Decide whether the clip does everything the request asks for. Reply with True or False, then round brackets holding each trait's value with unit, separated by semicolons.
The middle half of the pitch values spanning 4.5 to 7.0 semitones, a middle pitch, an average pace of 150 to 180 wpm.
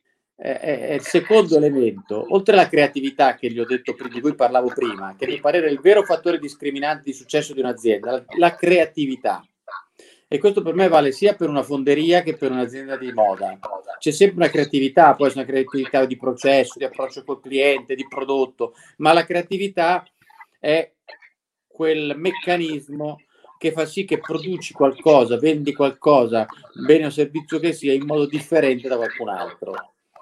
False (4.1 semitones; 150 Hz; 170 wpm)